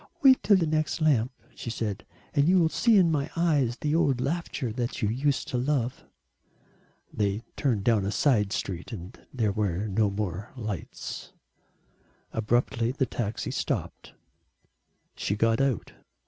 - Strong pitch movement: Yes, wide, 5.7 semitones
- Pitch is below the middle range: Yes, low, 120 Hz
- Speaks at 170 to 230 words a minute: No, average, 150 wpm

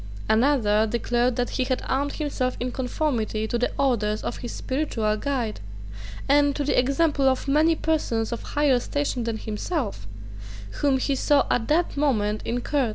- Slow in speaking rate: No, average, 165 wpm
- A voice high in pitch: Yes, very high, 255 Hz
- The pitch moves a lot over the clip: No, average, 4.0 semitones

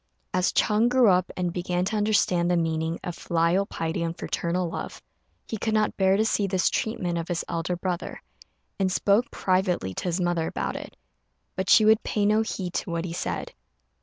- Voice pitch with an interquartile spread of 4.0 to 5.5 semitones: No, average, 3.2 semitones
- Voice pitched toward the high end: No, medium, 180 Hz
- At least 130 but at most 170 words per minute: No, average, 195 wpm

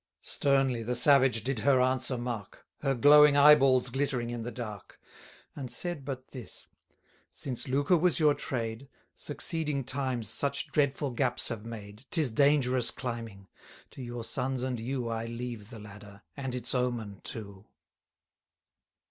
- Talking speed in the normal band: Yes, average, 150 wpm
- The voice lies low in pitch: Yes, low, 125 Hz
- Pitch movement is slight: No, average, 3.0 semitones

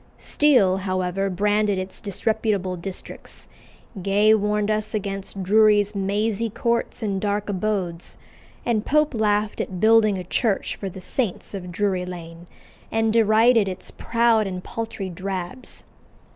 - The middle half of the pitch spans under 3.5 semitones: Yes, narrow, 2.5 semitones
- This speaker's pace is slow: Yes, slow, 130 wpm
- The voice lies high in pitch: Yes, high, 205 Hz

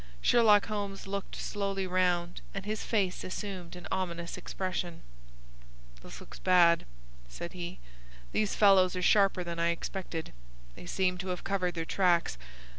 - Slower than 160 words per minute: Yes, average, 145 wpm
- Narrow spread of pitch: Yes, narrow, 2.1 semitones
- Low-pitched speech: No, medium, 185 Hz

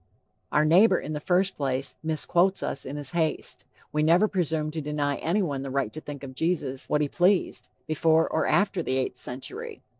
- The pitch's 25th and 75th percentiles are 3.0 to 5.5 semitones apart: Yes, average, 3.9 semitones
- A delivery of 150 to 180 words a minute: No, average, 190 wpm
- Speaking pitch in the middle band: Yes, medium, 155 Hz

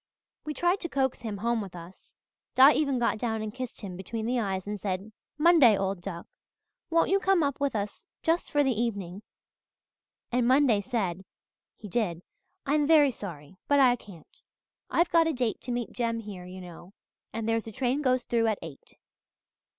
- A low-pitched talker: No, high, 230 Hz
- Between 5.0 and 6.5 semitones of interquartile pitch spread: Yes, wide, 5.6 semitones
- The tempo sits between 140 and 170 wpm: No, average, 190 wpm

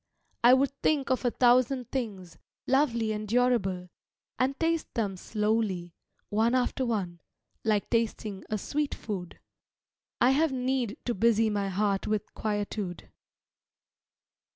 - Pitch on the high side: Yes, high, 225 Hz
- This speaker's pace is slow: Yes, slow, 130 wpm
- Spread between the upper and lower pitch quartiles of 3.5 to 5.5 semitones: Yes, average, 3.8 semitones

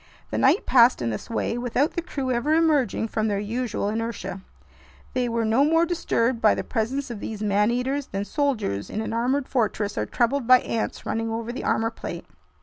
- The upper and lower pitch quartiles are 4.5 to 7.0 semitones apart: No, average, 3.3 semitones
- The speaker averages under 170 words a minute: No, average, 200 wpm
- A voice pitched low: No, high, 235 Hz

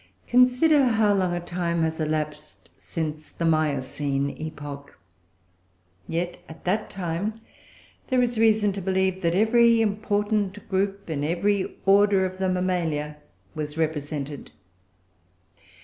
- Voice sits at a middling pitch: Yes, medium, 180 Hz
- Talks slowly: Yes, slow, 120 wpm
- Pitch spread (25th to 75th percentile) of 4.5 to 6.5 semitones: Yes, average, 5.0 semitones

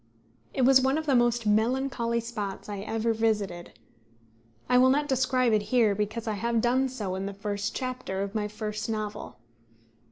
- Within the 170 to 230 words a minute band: Yes, average, 180 wpm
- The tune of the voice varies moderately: Yes, average, 3.4 semitones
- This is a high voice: Yes, high, 225 Hz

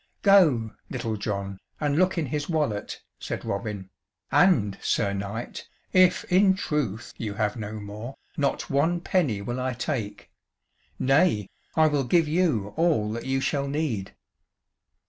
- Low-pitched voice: Yes, low, 130 Hz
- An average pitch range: No, wide, 7.0 semitones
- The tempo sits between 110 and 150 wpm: Yes, average, 145 wpm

